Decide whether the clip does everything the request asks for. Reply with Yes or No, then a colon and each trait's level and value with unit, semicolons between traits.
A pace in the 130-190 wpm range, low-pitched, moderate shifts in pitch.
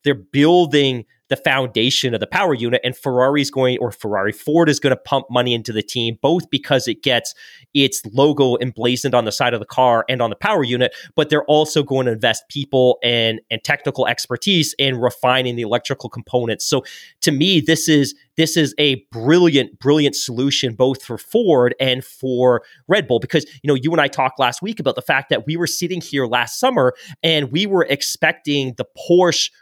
No: average, 200 wpm; low, 130 Hz; average, 3.3 semitones